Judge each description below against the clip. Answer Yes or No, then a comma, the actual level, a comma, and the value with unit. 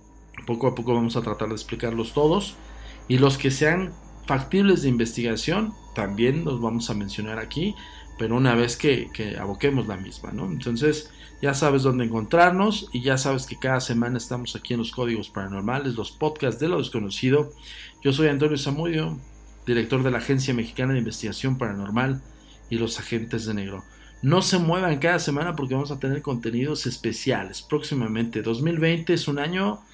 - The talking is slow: No, average, 170 wpm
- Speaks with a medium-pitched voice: No, low, 130 Hz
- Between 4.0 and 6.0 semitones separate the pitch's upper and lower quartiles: Yes, average, 4.4 semitones